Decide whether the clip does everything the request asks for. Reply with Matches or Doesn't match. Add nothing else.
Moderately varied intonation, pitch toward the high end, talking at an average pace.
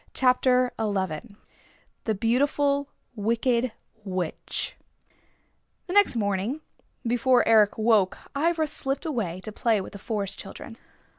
Doesn't match